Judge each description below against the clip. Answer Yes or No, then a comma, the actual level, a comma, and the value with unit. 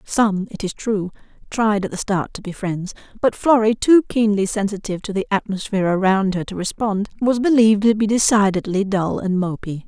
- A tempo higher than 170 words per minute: Yes, average, 190 wpm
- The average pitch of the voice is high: Yes, high, 205 Hz